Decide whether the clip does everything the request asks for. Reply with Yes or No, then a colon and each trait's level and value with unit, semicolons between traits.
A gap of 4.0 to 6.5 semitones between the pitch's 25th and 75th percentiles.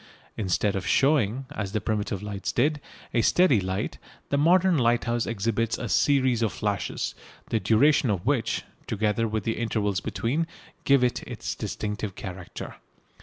Yes: average, 4.4 semitones